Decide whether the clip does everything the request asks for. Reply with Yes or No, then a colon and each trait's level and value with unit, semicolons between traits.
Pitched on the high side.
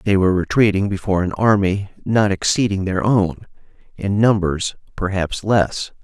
No: low, 100 Hz